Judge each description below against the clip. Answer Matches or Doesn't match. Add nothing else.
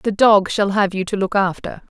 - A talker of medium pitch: Doesn't match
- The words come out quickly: Matches